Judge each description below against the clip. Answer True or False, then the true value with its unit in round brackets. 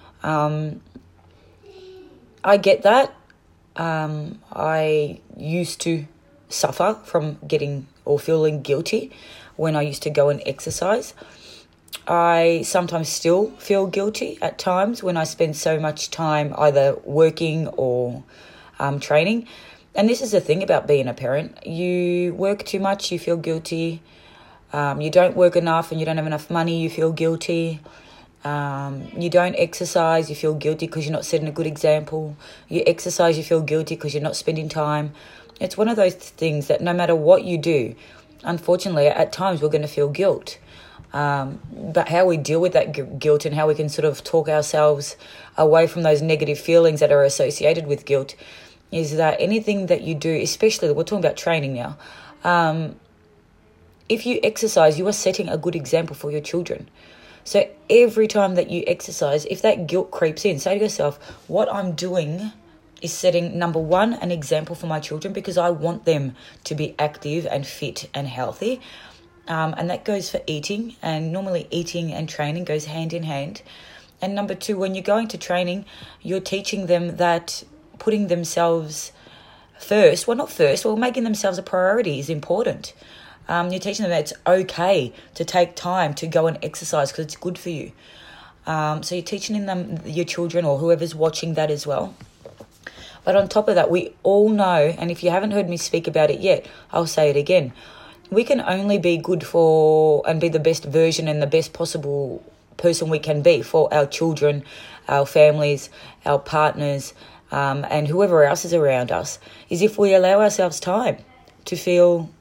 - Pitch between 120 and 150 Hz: False (165 Hz)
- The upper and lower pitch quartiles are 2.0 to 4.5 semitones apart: True (3.0 semitones)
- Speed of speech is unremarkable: True (180 wpm)